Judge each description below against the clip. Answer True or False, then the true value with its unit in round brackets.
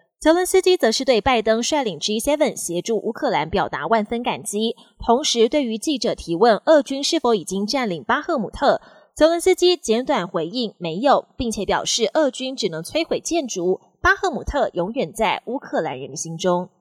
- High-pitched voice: True (235 Hz)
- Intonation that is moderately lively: False (6.5 semitones)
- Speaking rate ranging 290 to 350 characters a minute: False (280 characters per minute)